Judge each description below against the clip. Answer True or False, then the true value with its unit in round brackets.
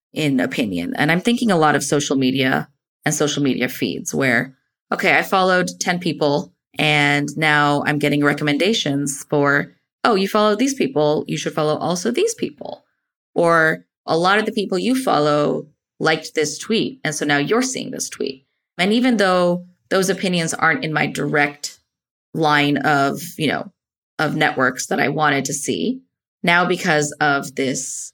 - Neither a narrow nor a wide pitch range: True (4.4 semitones)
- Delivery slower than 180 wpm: True (170 wpm)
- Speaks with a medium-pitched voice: True (150 Hz)